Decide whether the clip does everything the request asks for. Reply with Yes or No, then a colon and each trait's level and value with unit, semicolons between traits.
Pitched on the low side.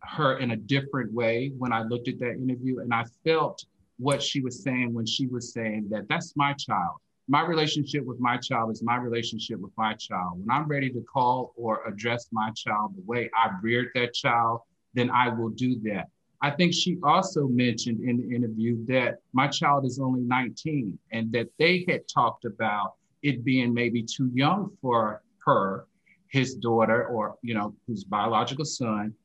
Yes: low, 125 Hz